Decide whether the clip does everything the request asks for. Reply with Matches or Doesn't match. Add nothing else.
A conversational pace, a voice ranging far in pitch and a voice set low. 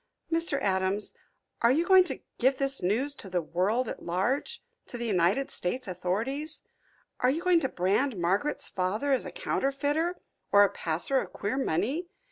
Doesn't match